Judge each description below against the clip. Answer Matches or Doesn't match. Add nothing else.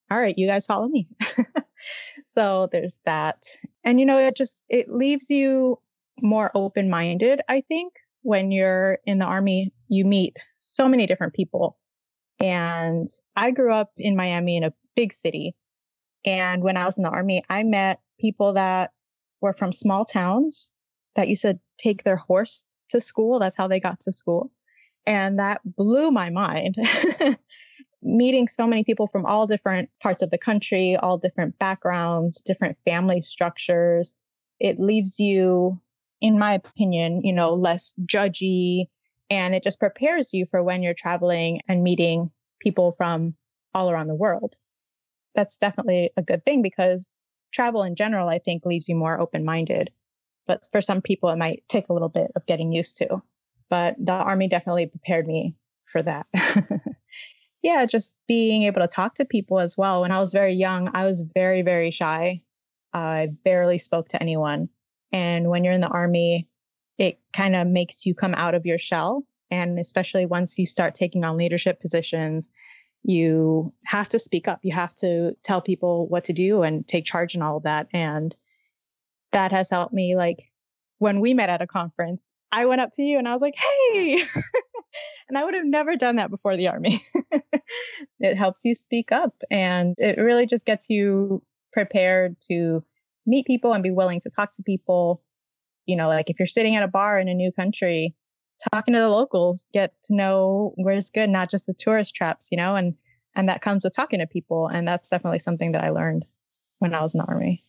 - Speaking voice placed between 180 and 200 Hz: Matches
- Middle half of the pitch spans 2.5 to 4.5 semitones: Matches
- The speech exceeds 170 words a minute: Matches